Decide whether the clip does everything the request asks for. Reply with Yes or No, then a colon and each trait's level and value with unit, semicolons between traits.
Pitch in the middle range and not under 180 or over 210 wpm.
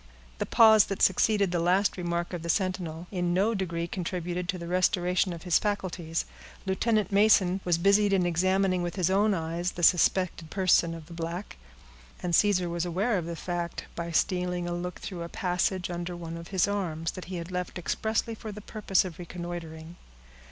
Yes: medium, 180 Hz; average, 190 wpm